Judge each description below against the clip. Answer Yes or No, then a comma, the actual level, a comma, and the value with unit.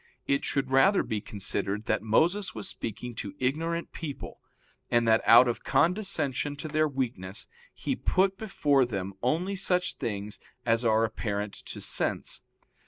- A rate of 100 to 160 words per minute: Yes, average, 150 wpm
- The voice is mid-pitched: No, low, 130 Hz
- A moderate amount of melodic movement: No, wide, 6.7 semitones